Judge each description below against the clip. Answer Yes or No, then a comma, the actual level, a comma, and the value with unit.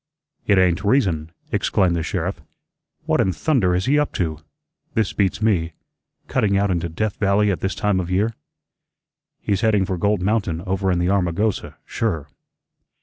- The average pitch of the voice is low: Yes, very low, 95 Hz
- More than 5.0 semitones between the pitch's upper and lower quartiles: No, average, 2.9 semitones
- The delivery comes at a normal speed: Yes, average, 165 wpm